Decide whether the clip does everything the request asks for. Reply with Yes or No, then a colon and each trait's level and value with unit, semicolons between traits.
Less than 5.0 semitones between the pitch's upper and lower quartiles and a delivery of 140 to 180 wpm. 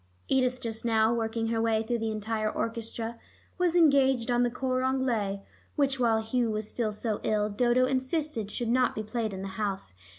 No: average, 2.7 semitones; average, 190 wpm